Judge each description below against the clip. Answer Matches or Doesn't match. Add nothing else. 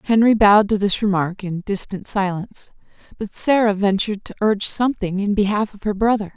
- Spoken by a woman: Matches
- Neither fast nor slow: Matches